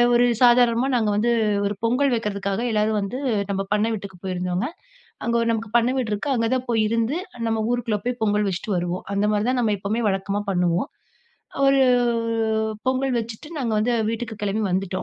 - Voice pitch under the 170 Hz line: No, high, 220 Hz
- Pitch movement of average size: Yes, average, 3.1 semitones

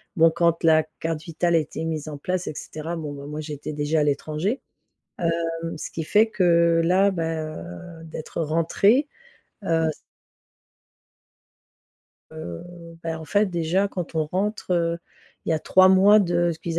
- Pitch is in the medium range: Yes, medium, 165 Hz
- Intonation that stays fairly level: Yes, narrow, 2.3 semitones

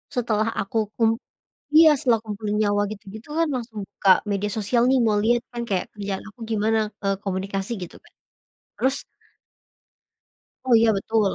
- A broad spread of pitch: No, narrow, 2.6 semitones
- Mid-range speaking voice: No, high, 215 Hz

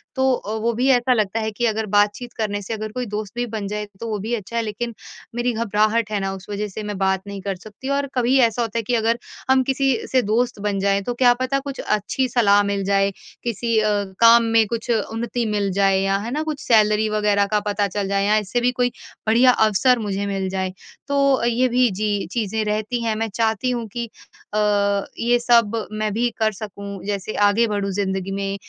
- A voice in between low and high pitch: No, high, 215 Hz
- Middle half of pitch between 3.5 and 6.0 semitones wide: No, average, 2.9 semitones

